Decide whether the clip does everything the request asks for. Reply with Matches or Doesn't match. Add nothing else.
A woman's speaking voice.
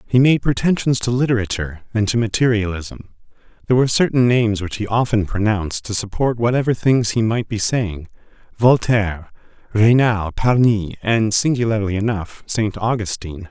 Doesn't match